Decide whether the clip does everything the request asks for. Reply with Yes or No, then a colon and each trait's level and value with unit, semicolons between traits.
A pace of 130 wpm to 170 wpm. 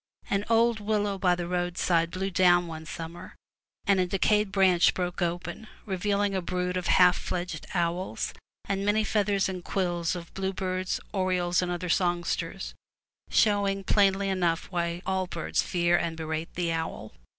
Yes: average, 155 wpm